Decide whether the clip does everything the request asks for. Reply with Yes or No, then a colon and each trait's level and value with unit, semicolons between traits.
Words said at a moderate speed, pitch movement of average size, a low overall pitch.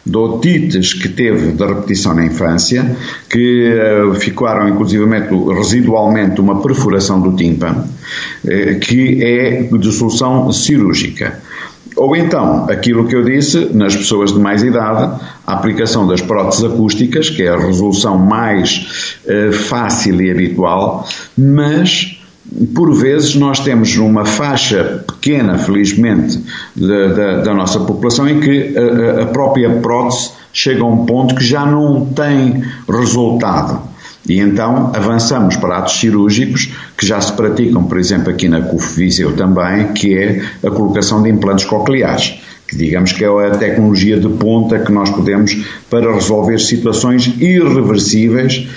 Yes: average, 140 wpm; average, 3.6 semitones; low, 110 Hz